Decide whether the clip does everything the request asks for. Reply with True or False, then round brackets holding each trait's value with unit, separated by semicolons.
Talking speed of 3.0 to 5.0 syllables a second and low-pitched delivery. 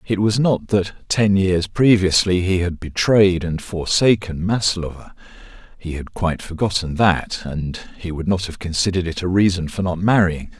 True (4.7 syllables/s; 90 Hz)